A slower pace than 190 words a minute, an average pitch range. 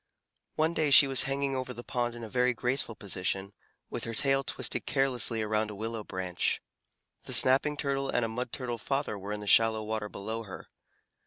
No: average, 195 wpm; average, 4.0 semitones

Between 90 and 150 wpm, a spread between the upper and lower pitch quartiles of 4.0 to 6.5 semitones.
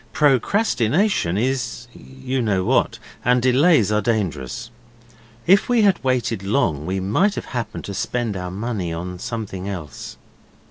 Yes: average, 140 wpm; wide, 5.5 semitones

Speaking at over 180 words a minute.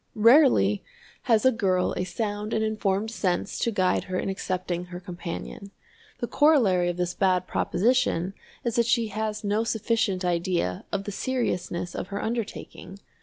No: average, 160 wpm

